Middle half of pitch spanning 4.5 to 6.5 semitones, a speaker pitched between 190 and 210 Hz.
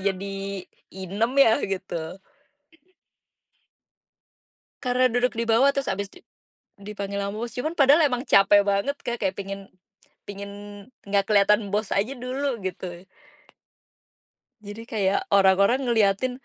No: average, 3.7 semitones; high, 205 Hz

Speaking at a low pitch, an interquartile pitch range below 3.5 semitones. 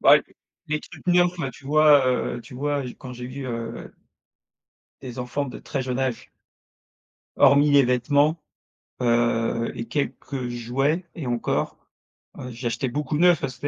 Yes: low, 130 Hz; average, 3.1 semitones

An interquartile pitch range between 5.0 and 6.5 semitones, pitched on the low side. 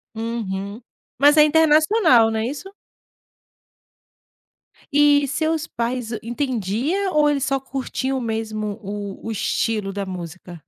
No: wide, 5.6 semitones; high, 240 Hz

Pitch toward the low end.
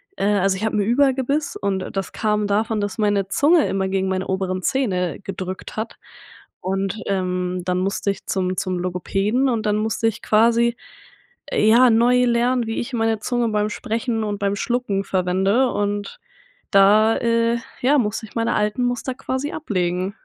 No: high, 210 Hz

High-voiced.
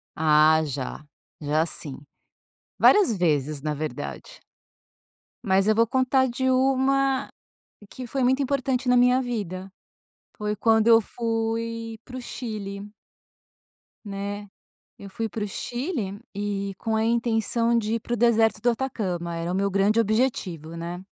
Yes: high, 220 Hz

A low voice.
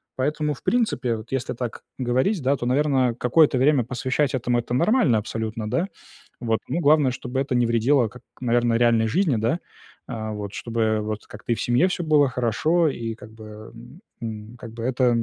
Yes: low, 125 Hz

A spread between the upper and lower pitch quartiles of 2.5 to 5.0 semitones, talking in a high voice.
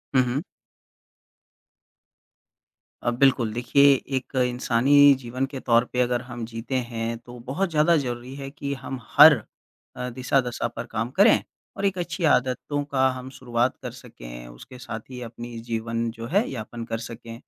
No: average, 2.8 semitones; low, 125 Hz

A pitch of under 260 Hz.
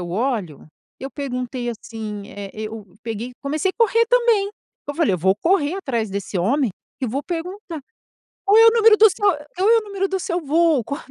No: very high, 290 Hz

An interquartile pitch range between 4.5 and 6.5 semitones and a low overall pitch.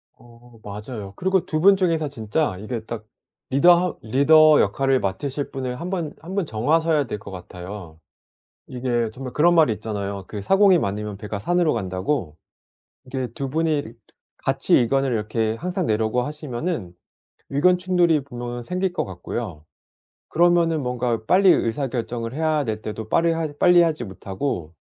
No: wide, 6.9 semitones; low, 130 Hz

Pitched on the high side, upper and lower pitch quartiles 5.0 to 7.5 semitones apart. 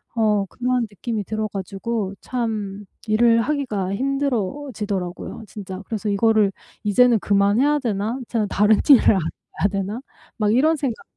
No: high, 215 Hz; average, 3.4 semitones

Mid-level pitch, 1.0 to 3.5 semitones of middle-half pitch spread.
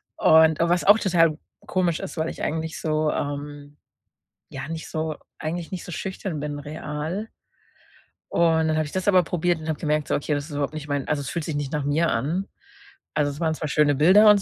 Yes: medium, 155 Hz; narrow, 2.6 semitones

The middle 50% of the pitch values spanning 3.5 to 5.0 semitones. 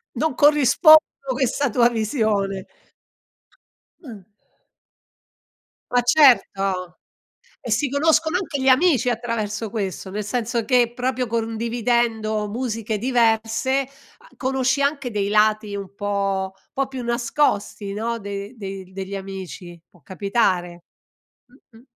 Yes: average, 4.3 semitones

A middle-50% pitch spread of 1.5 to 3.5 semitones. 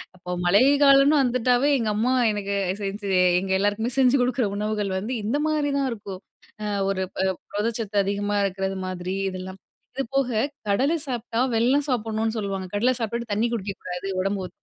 No: average, 4.1 semitones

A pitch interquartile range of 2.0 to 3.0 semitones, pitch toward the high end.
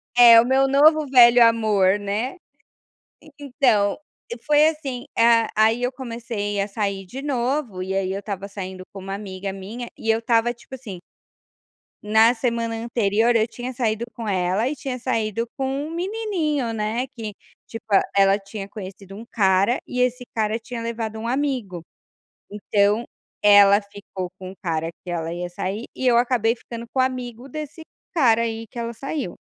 No: average, 3.7 semitones; high, 230 Hz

